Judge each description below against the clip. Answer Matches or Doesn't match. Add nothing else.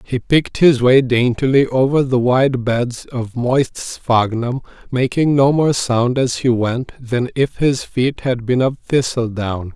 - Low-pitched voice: Matches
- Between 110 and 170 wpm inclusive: Matches